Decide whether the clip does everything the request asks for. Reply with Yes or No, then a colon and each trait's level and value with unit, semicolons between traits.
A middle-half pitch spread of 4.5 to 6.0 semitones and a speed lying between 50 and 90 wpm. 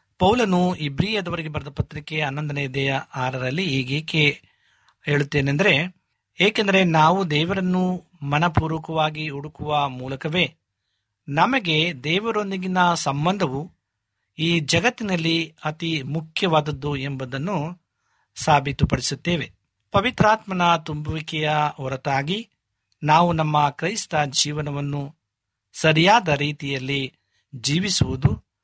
No: average, 3.9 semitones; average, 70 wpm